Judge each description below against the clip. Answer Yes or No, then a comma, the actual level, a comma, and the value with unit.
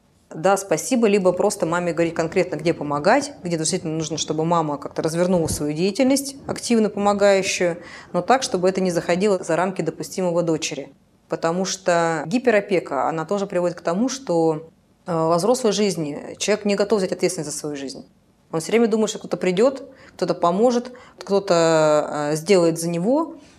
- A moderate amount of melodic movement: Yes, average, 3.9 semitones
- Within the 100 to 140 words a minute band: No, fast, 160 wpm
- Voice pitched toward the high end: No, medium, 180 Hz